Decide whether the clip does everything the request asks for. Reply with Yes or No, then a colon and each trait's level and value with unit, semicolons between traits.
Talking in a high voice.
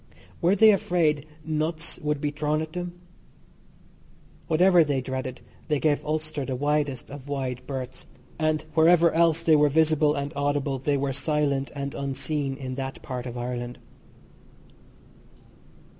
No: medium, 145 Hz